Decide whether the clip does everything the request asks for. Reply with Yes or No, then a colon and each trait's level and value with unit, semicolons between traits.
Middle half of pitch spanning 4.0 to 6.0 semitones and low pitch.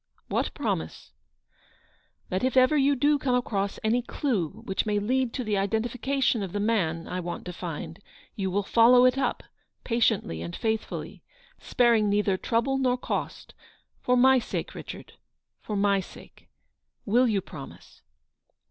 No: average, 4.4 semitones; high, 220 Hz